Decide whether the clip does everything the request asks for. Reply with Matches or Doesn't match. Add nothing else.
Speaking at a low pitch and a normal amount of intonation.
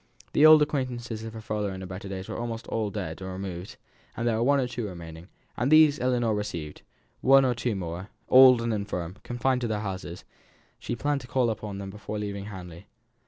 Matches